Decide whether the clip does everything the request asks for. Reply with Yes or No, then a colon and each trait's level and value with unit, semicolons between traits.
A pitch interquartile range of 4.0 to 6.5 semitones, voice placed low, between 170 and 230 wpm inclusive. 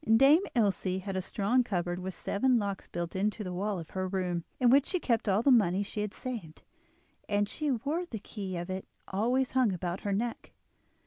No: average, 4.4 semitones; high, 205 Hz; fast, 205 wpm